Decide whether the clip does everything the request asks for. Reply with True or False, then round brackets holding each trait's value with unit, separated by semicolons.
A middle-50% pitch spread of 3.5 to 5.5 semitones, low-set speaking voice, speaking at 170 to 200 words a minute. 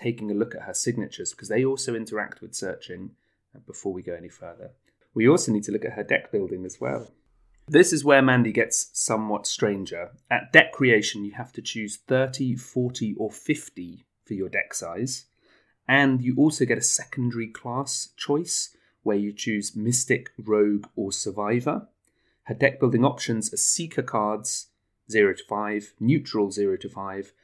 True (3.8 semitones; 115 Hz; 175 wpm)